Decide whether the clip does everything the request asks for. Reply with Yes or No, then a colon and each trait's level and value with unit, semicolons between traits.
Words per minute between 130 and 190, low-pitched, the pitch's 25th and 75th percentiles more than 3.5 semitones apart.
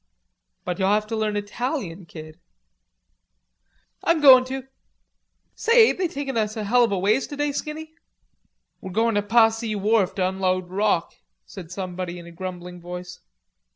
No: average, 155 wpm; high, 205 Hz; average, 5.2 semitones